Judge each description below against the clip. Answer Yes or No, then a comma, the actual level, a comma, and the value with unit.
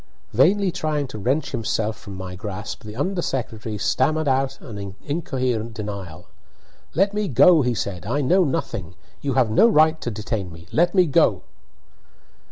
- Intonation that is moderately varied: No, wide, 6.8 semitones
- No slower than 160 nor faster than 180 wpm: Yes, average, 165 wpm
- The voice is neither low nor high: No, low, 125 Hz